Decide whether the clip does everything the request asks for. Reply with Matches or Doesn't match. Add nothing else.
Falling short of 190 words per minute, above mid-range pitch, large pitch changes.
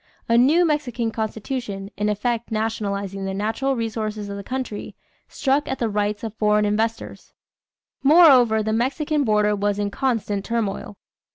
Doesn't match